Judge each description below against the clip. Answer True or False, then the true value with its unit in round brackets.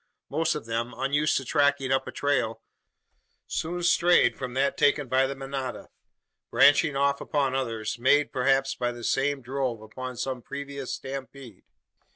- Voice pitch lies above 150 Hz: False (135 Hz)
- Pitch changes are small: True (2.1 semitones)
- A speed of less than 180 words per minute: True (155 wpm)